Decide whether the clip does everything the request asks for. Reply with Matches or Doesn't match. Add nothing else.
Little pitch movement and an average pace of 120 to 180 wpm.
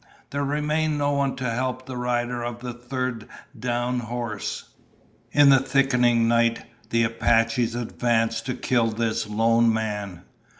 Matches